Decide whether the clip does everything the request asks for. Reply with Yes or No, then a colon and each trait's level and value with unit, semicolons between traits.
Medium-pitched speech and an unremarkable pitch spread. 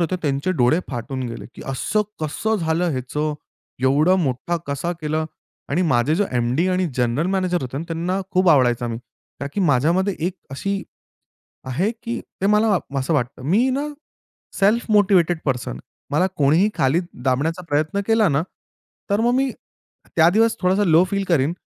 No: medium, 165 Hz; wide, 5.7 semitones